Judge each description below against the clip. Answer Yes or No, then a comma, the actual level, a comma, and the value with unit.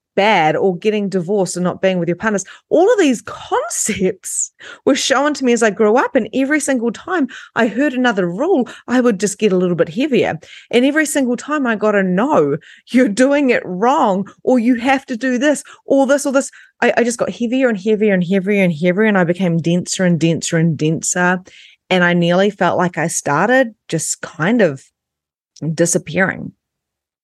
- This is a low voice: No, high, 210 Hz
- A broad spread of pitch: Yes, wide, 6.3 semitones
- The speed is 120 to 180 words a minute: No, average, 195 wpm